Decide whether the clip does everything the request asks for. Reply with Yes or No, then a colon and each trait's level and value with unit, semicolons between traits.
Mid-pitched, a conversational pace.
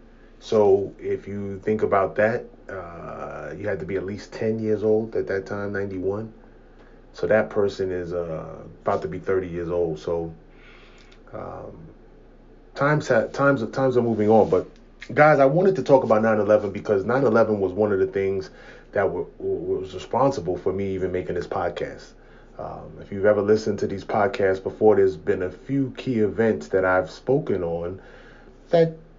No: low, 110 Hz; average, 175 wpm